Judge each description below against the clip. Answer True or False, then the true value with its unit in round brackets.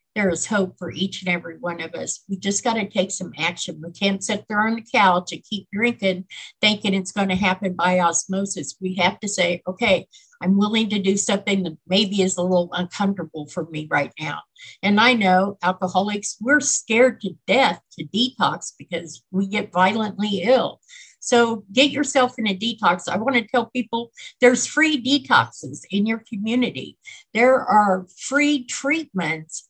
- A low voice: False (200 Hz)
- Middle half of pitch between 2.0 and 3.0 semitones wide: False (4.3 semitones)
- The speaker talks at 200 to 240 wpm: False (180 wpm)